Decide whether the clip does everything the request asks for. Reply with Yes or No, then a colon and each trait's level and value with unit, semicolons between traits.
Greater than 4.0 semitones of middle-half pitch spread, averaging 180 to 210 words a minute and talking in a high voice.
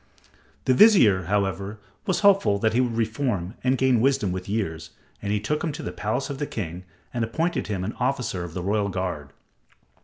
No: wide, 5.5 semitones; average, 195 wpm; low, 110 Hz